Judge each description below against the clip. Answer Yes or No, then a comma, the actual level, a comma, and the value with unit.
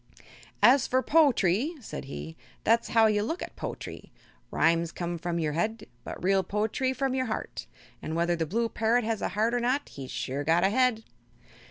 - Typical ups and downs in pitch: No, wide, 6.3 semitones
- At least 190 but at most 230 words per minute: Yes, average, 195 wpm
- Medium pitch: No, high, 215 Hz